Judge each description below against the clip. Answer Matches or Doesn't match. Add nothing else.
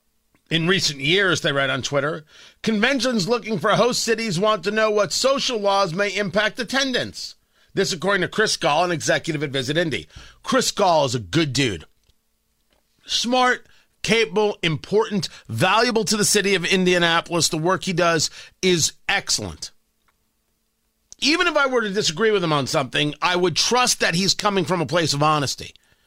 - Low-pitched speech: Doesn't match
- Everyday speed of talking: Matches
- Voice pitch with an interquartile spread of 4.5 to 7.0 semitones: Matches